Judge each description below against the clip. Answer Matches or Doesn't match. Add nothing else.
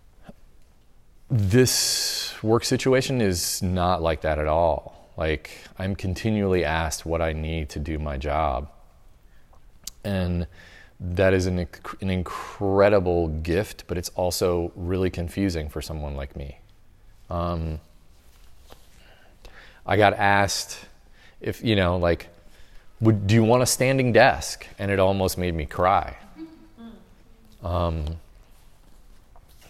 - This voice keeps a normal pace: Doesn't match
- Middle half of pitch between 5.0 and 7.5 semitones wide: Doesn't match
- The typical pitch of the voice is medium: Doesn't match